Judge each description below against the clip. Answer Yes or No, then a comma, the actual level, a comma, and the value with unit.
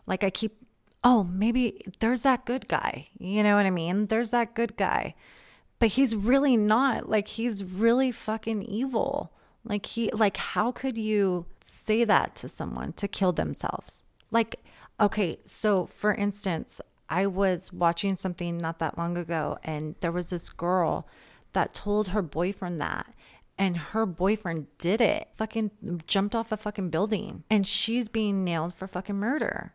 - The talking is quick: No, average, 165 wpm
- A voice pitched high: Yes, high, 205 Hz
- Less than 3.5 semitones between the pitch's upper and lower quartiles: No, average, 3.8 semitones